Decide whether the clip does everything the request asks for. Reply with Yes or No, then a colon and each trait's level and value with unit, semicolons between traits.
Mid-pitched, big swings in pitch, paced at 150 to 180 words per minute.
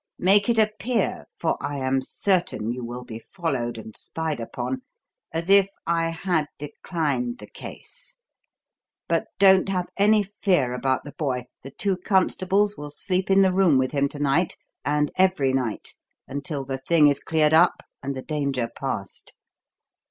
Yes: medium, 155 Hz; wide, 6.1 semitones; average, 160 wpm